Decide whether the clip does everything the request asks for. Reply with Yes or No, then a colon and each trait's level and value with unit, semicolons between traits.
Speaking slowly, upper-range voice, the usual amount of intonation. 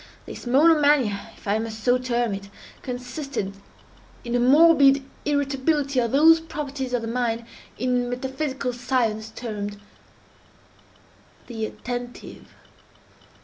Yes: slow, 110 wpm; very high, 250 Hz; average, 3.2 semitones